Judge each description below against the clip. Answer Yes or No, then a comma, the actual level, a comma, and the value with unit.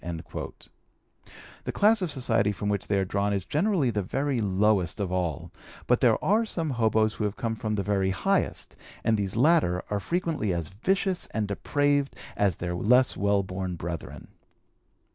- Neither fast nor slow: Yes, average, 175 wpm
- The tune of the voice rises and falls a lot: Yes, wide, 6.9 semitones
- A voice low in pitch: Yes, low, 105 Hz